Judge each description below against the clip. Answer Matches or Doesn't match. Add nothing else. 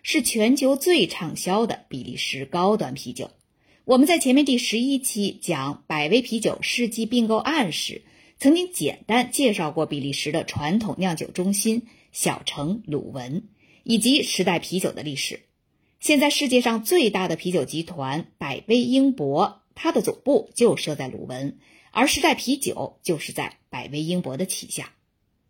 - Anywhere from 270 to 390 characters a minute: Doesn't match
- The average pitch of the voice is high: Matches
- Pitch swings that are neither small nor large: Doesn't match